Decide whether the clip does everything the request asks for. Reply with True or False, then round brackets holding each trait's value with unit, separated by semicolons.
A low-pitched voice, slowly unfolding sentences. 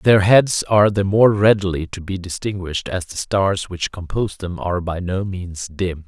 False (95 Hz; 195 wpm)